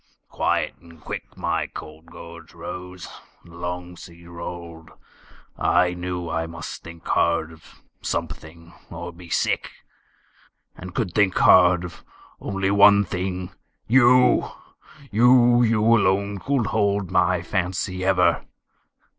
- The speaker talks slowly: Yes, slow, 120 wpm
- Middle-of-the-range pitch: No, very low, 90 Hz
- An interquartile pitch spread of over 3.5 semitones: No, average, 2.9 semitones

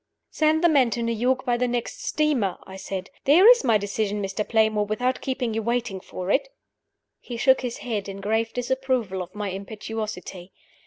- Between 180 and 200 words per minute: Yes, average, 190 wpm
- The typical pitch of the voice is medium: No, high, 225 Hz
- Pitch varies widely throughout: No, average, 4.0 semitones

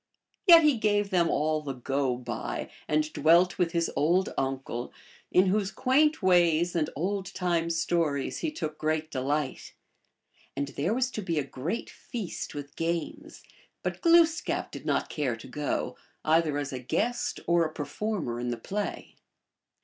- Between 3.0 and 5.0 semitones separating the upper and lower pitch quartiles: No, wide, 5.4 semitones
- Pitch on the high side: No, medium, 165 Hz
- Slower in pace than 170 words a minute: Yes, average, 160 wpm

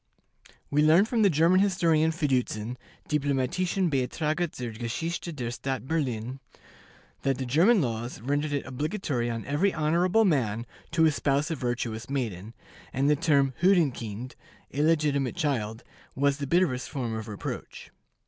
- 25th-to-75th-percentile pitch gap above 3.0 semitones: Yes, average, 4.8 semitones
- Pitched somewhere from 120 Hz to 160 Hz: Yes, medium, 140 Hz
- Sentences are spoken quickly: No, average, 140 wpm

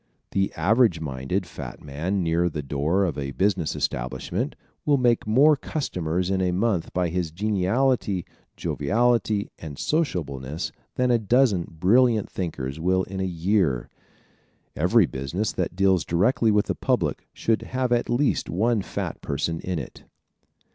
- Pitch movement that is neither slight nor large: No, wide, 5.8 semitones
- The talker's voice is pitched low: Yes, very low, 95 Hz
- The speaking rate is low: No, average, 150 wpm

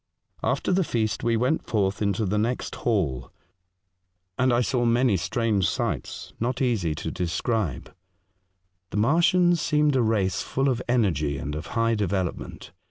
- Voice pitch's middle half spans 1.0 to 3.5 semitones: No, average, 4.7 semitones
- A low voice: Yes, low, 115 Hz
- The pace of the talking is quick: No, average, 165 wpm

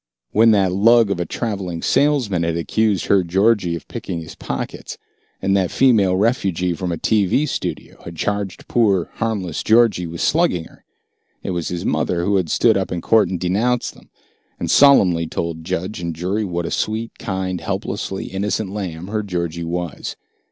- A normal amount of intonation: Yes, average, 3.9 semitones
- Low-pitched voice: Yes, very low, 95 Hz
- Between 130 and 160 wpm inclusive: No, average, 175 wpm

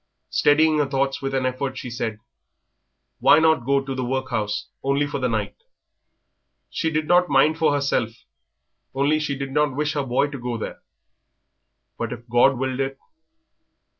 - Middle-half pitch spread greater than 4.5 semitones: No, narrow, 2.5 semitones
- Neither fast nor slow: Yes, average, 165 wpm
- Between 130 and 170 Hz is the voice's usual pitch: Yes, low, 135 Hz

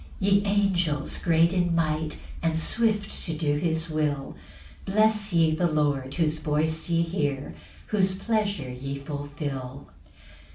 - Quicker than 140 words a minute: No, slow, 135 wpm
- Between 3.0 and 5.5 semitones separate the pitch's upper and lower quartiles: Yes, average, 4.4 semitones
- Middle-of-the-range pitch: Yes, medium, 160 Hz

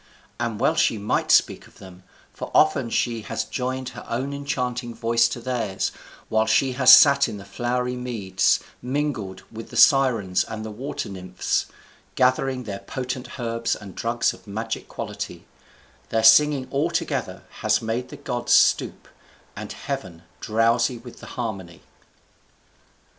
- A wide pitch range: No, average, 2.9 semitones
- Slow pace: No, average, 150 wpm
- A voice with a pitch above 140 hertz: No, low, 120 Hz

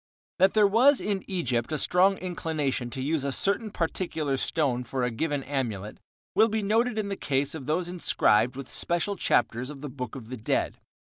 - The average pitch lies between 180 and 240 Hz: No, medium, 150 Hz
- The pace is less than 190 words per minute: No, average, 195 wpm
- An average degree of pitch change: No, wide, 6.9 semitones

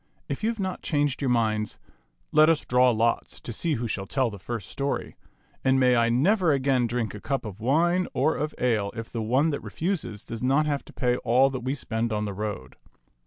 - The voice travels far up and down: No, average, 4.4 semitones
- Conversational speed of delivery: No, fast, 220 wpm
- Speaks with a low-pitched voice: Yes, low, 125 Hz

